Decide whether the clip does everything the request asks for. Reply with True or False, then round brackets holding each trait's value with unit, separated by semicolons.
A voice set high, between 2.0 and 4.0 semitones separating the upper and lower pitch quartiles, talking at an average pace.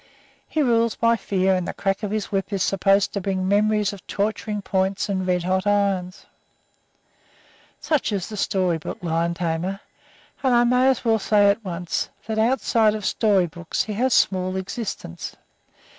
True (200 Hz; 2.7 semitones; 175 wpm)